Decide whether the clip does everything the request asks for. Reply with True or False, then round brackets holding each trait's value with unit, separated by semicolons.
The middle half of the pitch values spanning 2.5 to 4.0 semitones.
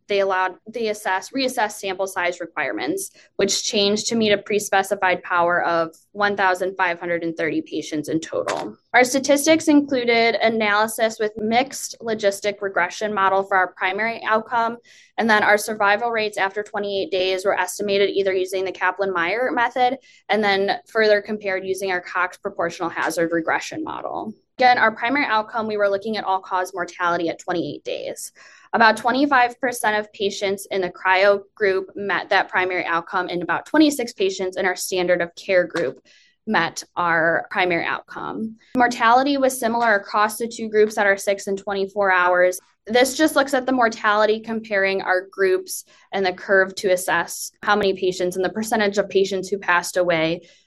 True (3.3 semitones)